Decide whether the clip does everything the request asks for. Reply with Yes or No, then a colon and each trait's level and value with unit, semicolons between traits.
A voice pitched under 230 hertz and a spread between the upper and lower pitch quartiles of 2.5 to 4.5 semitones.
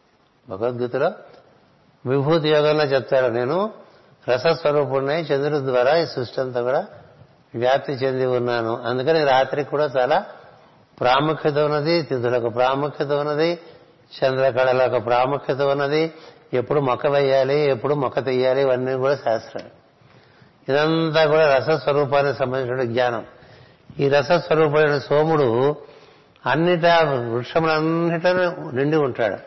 Yes: medium, 140 Hz; average, 3.3 semitones